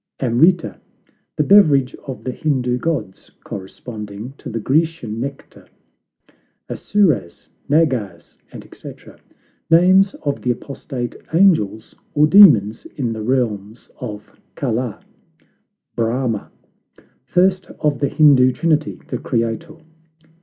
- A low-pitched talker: Yes, low, 130 Hz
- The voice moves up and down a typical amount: No, wide, 5.7 semitones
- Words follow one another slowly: Yes, slow, 105 wpm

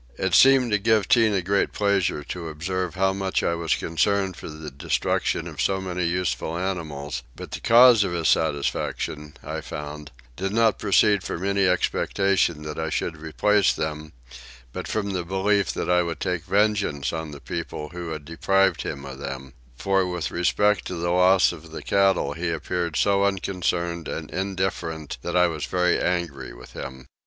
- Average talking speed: Yes, average, 180 wpm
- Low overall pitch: Yes, very low, 90 Hz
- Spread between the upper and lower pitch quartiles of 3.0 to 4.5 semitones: Yes, average, 3.6 semitones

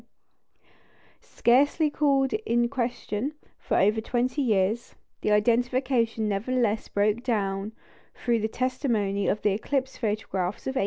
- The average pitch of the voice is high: Yes, high, 235 Hz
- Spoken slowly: Yes, slow, 120 wpm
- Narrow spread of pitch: No, average, 3.5 semitones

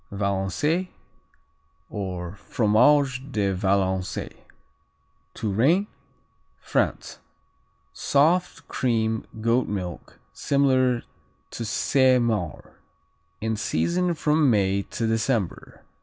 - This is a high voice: No, low, 115 Hz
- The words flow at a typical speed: No, slow, 80 wpm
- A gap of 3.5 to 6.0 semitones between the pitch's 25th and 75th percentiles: Yes, wide, 5.6 semitones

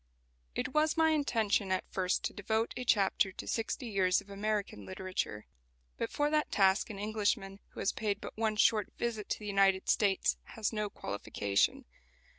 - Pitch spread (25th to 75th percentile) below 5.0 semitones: Yes, narrow, 2.6 semitones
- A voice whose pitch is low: No, high, 205 Hz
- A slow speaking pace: No, average, 175 wpm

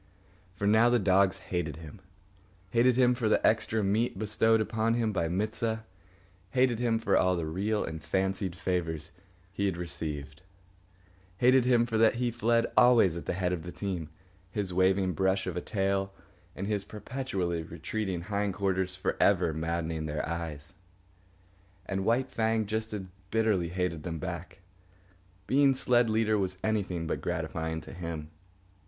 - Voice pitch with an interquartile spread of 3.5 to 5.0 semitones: Yes, average, 4.1 semitones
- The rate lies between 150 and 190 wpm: Yes, average, 160 wpm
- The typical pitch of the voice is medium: No, very low, 95 Hz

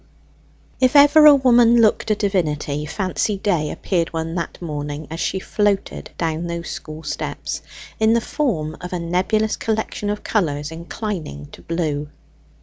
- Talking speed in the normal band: Yes, average, 150 wpm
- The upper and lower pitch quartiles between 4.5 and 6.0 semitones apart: Yes, wide, 5.5 semitones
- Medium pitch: Yes, medium, 180 Hz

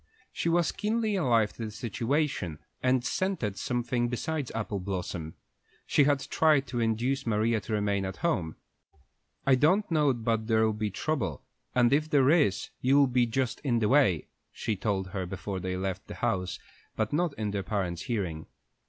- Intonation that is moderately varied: No, wide, 5.7 semitones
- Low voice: Yes, low, 115 Hz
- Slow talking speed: No, average, 170 wpm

